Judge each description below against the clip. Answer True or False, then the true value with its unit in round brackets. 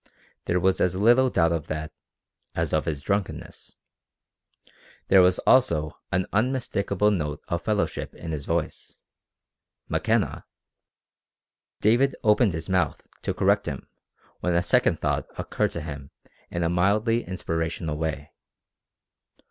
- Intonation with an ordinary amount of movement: True (4.3 semitones)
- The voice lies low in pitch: True (90 Hz)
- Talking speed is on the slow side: True (130 wpm)